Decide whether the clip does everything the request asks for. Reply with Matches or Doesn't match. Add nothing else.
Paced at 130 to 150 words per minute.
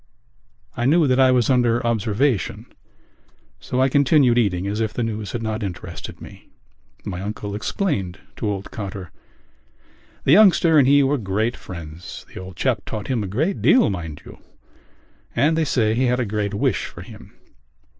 Doesn't match